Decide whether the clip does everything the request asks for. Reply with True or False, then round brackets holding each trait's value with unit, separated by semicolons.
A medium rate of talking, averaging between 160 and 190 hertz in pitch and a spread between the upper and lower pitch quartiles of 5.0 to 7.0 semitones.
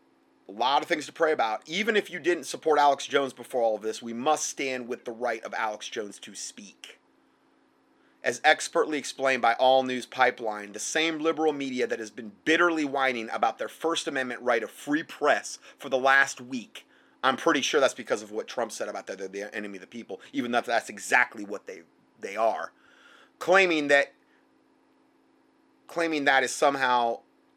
False (190 wpm; 140 Hz; 5.3 semitones)